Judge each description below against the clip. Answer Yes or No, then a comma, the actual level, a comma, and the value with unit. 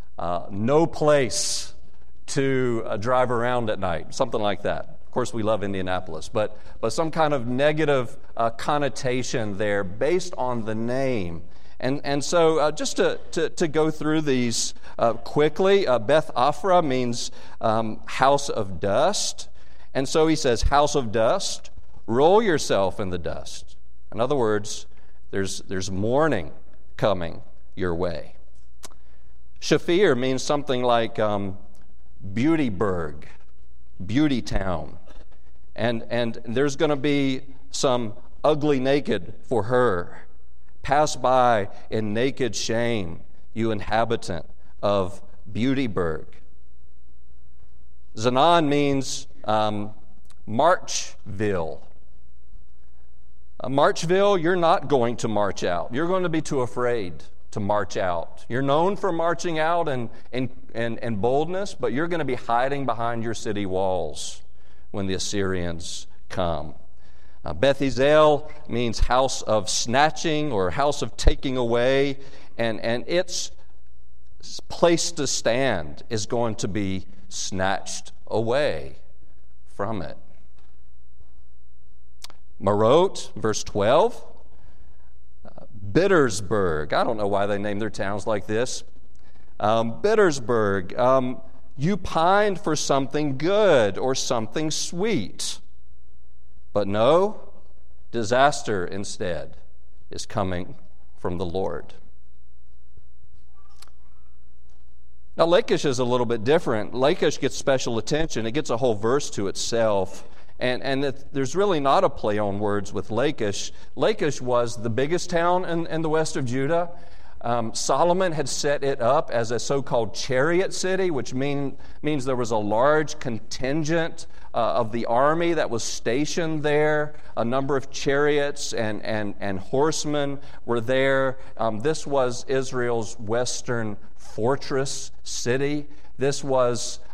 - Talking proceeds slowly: Yes, slow, 125 wpm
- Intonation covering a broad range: Yes, wide, 8.9 semitones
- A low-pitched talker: Yes, low, 115 Hz